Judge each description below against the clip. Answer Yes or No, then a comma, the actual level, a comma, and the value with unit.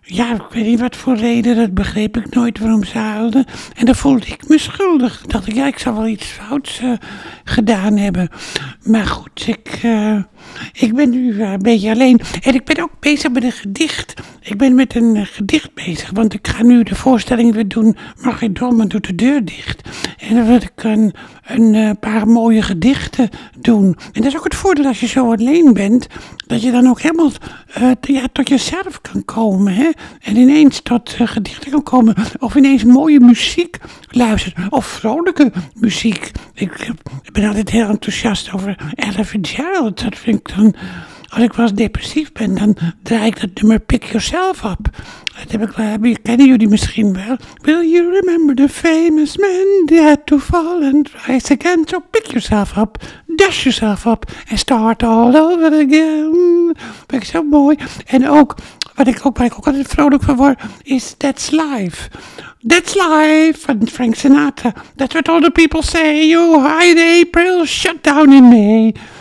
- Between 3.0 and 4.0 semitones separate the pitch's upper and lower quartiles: No, average, 5.0 semitones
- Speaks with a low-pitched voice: No, high, 245 Hz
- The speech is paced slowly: No, average, 185 wpm